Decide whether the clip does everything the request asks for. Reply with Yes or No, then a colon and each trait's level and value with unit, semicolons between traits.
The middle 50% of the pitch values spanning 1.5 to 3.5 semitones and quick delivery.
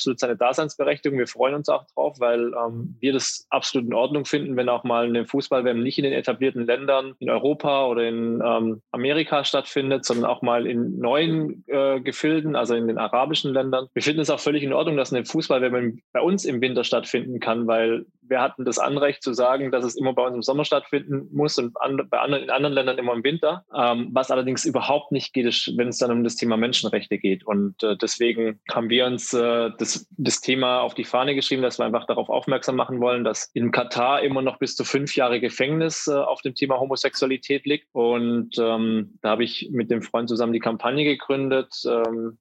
Yes: average, 2.8 semitones; fast, 215 wpm